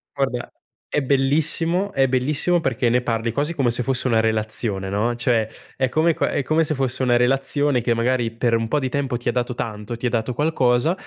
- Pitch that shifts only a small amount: No, average, 3.3 semitones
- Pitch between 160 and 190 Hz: No, low, 125 Hz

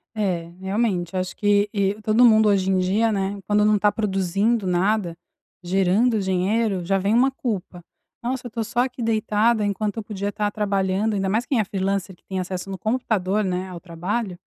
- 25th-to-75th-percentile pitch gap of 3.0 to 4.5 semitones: No, narrow, 2.5 semitones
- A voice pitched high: Yes, high, 200 Hz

